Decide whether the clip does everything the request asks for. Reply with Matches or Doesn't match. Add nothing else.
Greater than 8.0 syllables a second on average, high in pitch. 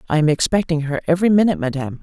Doesn't match